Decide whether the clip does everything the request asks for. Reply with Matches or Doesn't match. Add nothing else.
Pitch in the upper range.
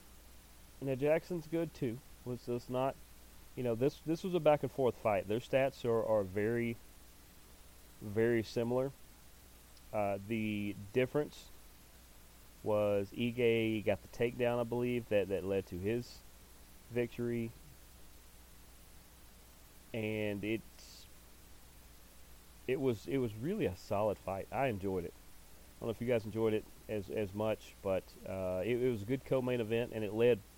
Doesn't match